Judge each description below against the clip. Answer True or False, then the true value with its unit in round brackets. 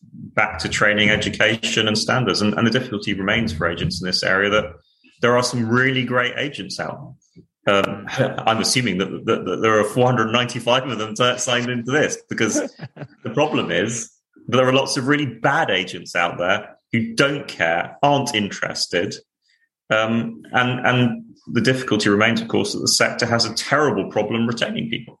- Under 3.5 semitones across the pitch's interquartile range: True (2.8 semitones)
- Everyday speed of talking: True (180 wpm)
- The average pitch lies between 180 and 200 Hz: False (120 Hz)